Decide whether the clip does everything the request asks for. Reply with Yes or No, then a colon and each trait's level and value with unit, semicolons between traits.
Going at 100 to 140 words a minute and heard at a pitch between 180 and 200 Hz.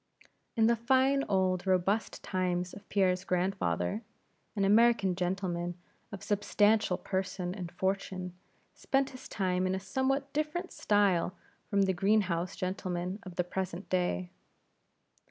Yes: slow, 135 wpm; high, 190 Hz